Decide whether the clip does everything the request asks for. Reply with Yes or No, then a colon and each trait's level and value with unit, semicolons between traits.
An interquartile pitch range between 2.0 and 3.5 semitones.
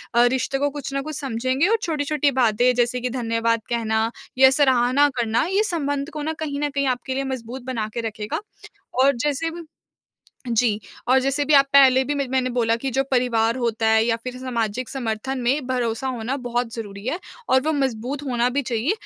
Yes: average, 3.1 semitones